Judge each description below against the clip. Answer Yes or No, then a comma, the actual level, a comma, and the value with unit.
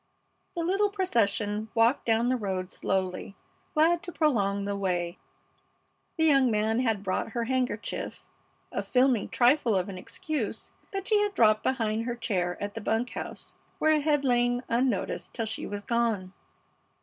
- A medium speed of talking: Yes, average, 160 wpm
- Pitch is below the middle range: No, high, 230 Hz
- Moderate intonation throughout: Yes, average, 4.6 semitones